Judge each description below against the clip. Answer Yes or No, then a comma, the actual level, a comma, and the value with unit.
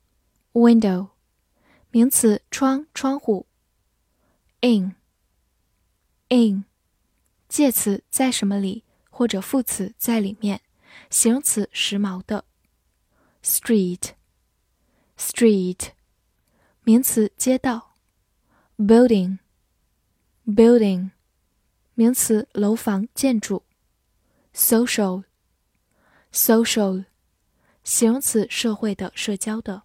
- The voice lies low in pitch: No, high, 215 Hz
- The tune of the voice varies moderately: Yes, average, 3.5 semitones